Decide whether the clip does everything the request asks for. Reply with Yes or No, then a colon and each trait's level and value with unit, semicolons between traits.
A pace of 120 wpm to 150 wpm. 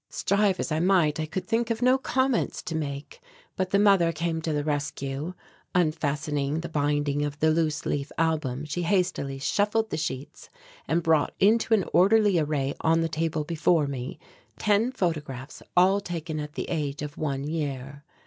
No: average, 175 wpm